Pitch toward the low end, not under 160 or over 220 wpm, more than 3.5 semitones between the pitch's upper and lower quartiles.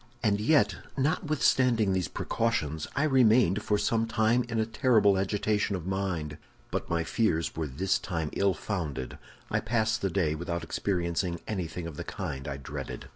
Yes: low, 100 Hz; average, 165 wpm; average, 5.0 semitones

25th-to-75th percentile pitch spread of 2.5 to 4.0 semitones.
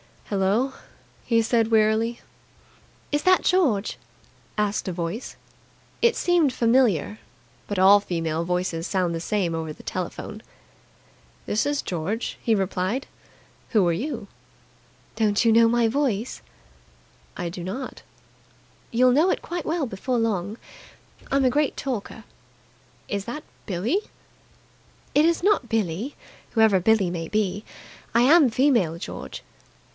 No: wide, 5.4 semitones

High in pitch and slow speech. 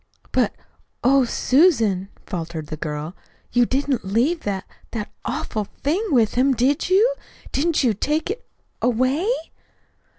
Yes: very high, 250 Hz; slow, 130 wpm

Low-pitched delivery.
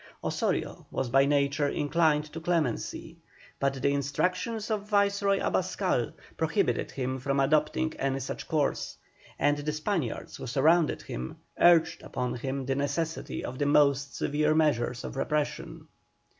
No: medium, 145 Hz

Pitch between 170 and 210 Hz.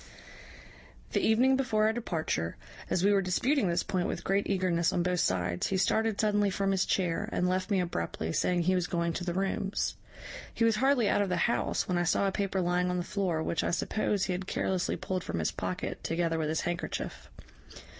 Yes: medium, 185 Hz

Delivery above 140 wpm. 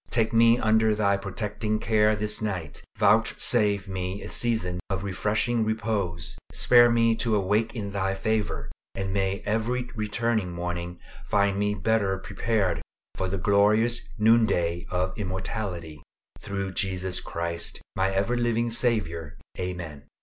No: slow, 135 wpm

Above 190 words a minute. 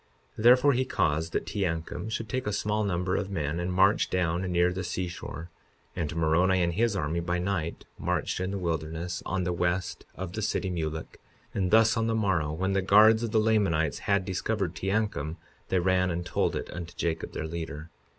Yes: average, 200 wpm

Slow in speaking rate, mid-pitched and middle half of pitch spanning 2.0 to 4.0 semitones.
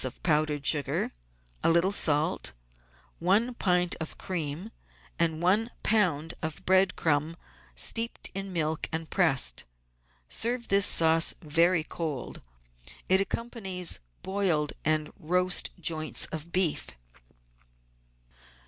Yes: slow, 110 wpm; medium, 170 Hz; average, 3.5 semitones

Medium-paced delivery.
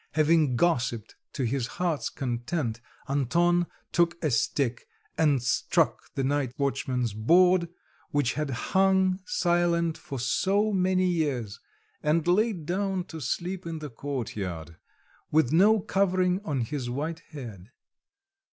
No: slow, 125 wpm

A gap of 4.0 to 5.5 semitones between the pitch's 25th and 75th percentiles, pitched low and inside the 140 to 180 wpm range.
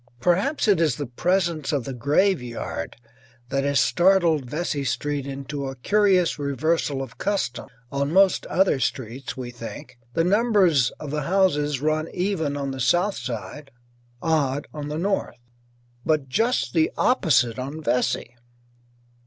No: average, 4.8 semitones; medium, 150 Hz; average, 145 wpm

